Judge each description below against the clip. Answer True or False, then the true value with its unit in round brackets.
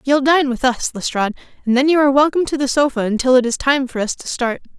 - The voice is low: False (265 Hz)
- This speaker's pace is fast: True (265 wpm)